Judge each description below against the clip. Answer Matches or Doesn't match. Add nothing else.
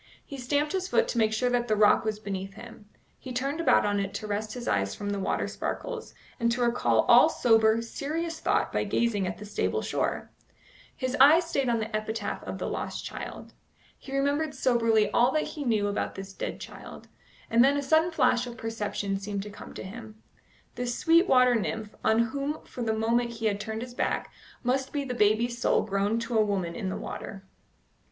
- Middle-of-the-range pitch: Doesn't match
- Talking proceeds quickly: Matches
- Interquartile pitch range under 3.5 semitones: Doesn't match